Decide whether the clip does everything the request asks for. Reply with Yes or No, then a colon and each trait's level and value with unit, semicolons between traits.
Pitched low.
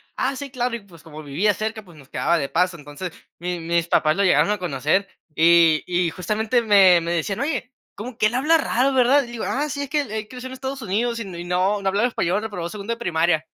No: high, 200 Hz